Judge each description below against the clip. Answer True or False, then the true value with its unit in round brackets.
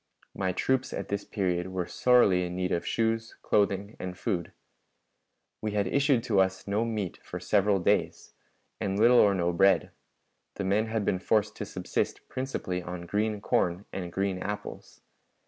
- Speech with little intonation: False (3.0 semitones)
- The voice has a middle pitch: False (100 Hz)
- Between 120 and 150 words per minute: False (170 wpm)